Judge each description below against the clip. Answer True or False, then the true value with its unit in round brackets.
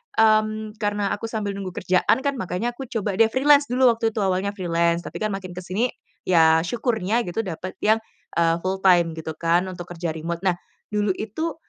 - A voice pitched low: False (200 Hz)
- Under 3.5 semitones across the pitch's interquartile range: False (4.1 semitones)